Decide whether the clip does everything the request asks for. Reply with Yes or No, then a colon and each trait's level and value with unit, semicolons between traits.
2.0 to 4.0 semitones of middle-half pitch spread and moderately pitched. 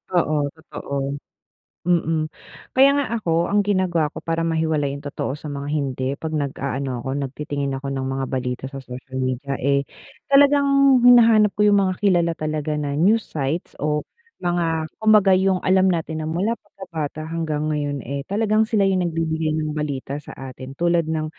No: average, 4.8 semitones; medium, 160 Hz